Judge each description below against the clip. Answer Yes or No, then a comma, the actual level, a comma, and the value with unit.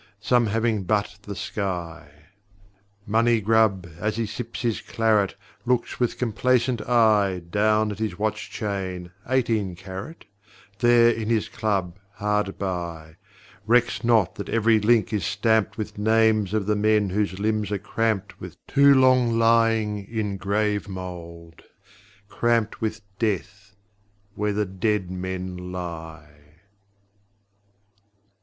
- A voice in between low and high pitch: No, low, 105 Hz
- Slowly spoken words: Yes, slow, 125 wpm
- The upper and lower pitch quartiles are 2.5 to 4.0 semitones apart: Yes, average, 3.0 semitones